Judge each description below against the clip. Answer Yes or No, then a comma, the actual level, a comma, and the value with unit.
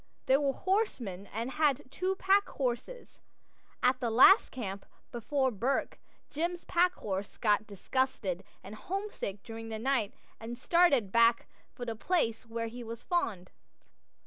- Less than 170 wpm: Yes, average, 140 wpm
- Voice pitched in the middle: No, high, 245 Hz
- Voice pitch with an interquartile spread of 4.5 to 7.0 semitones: Yes, wide, 5.6 semitones